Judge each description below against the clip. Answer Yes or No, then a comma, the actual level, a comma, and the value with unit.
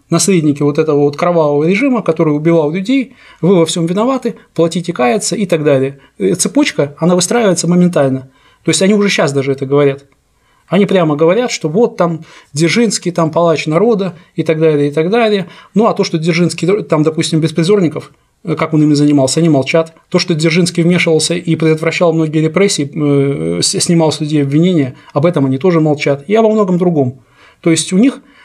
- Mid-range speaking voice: Yes, medium, 165 Hz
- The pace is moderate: No, fast, 180 wpm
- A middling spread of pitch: Yes, average, 3.7 semitones